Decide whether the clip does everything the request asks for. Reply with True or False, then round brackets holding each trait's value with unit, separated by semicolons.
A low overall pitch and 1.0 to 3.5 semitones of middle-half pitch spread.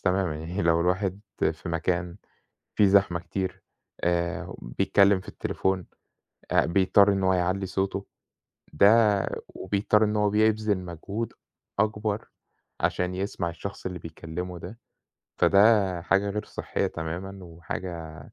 True (95 Hz; 2.7 semitones)